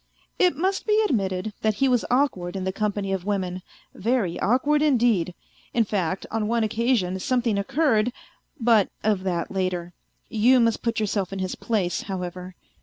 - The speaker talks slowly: No, average, 165 wpm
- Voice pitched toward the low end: No, high, 210 Hz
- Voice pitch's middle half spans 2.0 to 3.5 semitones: No, average, 4.5 semitones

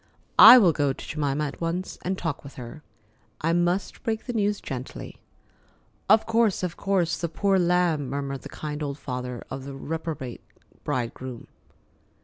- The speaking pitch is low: No, medium, 160 Hz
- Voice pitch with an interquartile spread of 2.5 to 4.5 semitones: No, average, 5.1 semitones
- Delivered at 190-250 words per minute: No, average, 155 wpm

